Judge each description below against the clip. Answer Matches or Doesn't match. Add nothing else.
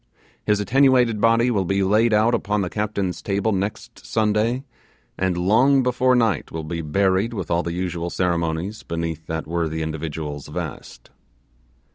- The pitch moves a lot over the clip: Doesn't match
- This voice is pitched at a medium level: Doesn't match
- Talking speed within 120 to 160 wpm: Matches